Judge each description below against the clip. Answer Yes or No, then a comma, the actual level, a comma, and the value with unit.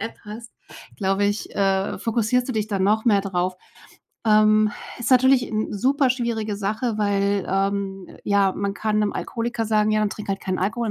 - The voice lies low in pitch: No, high, 210 Hz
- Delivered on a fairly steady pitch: Yes, narrow, 2.3 semitones